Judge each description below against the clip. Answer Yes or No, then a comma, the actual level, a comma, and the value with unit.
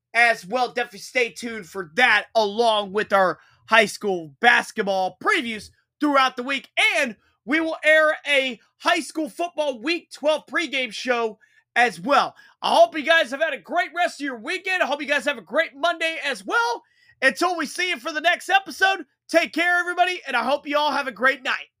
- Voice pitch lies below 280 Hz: No, very high, 285 Hz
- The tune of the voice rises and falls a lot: Yes, wide, 5.8 semitones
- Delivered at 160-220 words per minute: Yes, average, 200 wpm